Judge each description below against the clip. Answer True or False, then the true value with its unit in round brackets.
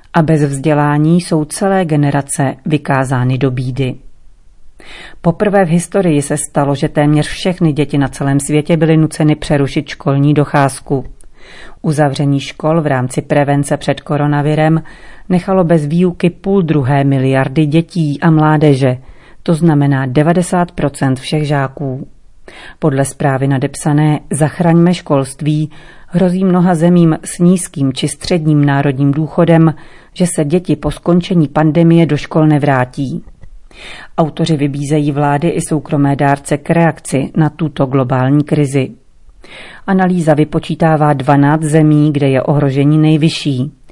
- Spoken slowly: False (125 wpm)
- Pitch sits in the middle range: True (150 Hz)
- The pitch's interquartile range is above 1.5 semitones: True (2.8 semitones)